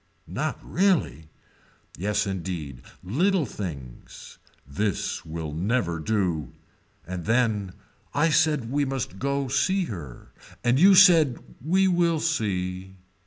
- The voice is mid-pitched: No, low, 110 Hz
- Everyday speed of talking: No, slow, 120 wpm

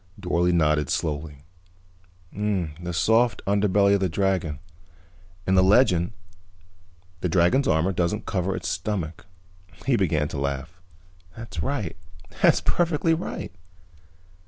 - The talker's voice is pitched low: Yes, very low, 90 Hz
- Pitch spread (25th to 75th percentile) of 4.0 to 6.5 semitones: Yes, average, 4.3 semitones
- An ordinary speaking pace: No, slow, 115 wpm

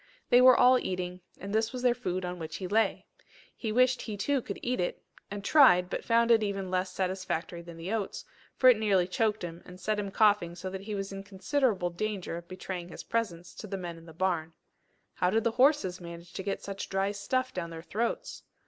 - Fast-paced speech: Yes, fast, 225 wpm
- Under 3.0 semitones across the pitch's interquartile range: No, average, 3.9 semitones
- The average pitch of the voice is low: No, high, 195 Hz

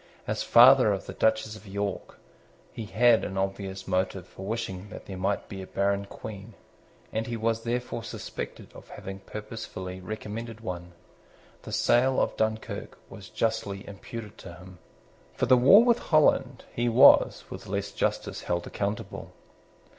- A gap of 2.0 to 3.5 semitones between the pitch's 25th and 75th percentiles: Yes, average, 2.9 semitones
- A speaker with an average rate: Yes, average, 155 wpm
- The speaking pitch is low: Yes, low, 105 Hz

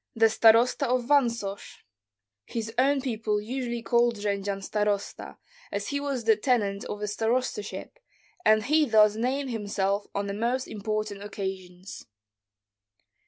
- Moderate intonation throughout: Yes, average, 3.3 semitones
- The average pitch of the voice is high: Yes, high, 220 Hz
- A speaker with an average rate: No, slow, 130 wpm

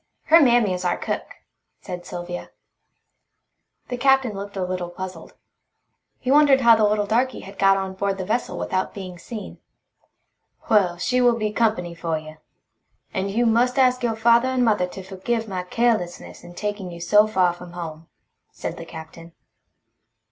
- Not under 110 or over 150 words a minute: No, average, 170 wpm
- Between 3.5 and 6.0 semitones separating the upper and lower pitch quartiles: Yes, average, 4.8 semitones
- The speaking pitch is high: Yes, high, 200 Hz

